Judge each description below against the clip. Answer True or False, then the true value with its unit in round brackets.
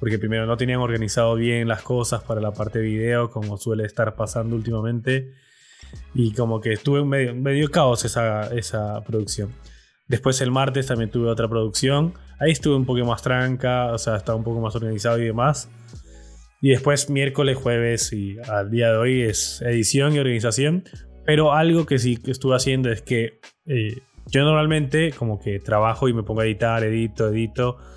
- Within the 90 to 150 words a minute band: False (180 wpm)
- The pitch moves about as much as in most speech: True (3.0 semitones)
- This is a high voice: False (120 Hz)